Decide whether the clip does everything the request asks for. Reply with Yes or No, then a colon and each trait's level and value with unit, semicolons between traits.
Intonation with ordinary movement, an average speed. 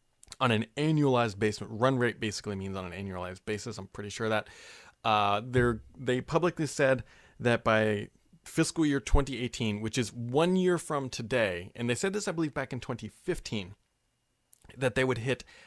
Yes: average, 3.7 semitones; average, 170 wpm